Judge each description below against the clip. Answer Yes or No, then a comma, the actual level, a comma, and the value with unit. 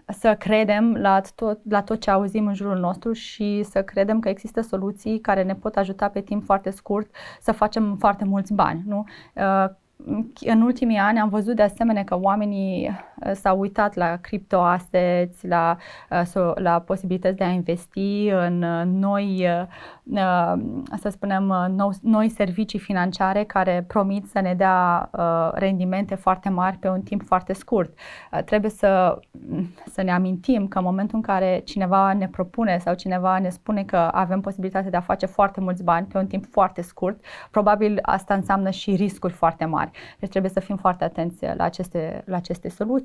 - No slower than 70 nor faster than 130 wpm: No, average, 165 wpm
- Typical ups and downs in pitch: No, narrow, 2.1 semitones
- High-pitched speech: Yes, high, 195 Hz